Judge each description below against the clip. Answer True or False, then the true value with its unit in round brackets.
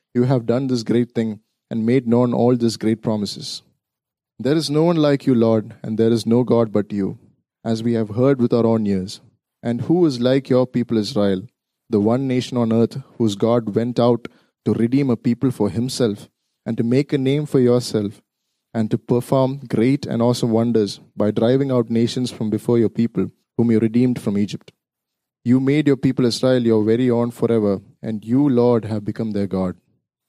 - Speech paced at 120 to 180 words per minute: False (200 wpm)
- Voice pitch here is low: True (120 Hz)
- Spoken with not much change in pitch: True (2.3 semitones)